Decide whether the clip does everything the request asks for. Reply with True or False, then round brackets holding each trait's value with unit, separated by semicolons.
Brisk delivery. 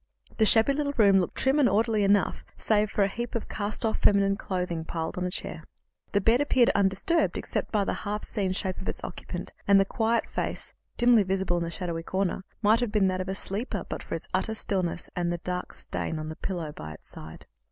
True (230 wpm)